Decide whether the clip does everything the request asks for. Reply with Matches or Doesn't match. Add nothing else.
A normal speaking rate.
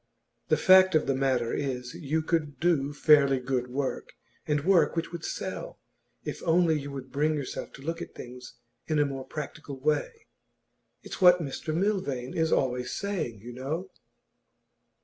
Matches